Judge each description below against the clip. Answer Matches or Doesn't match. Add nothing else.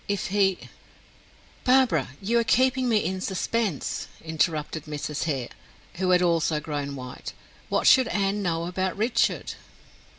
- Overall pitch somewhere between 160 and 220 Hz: Matches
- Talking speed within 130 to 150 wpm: Matches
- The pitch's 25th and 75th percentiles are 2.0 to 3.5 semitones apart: Doesn't match